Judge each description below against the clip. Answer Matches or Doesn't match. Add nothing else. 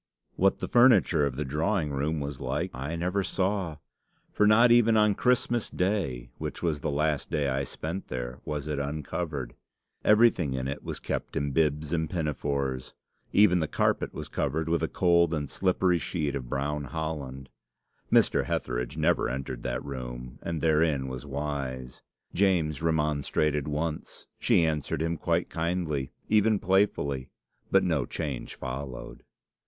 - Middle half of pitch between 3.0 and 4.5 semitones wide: Matches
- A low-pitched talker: Matches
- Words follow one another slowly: Doesn't match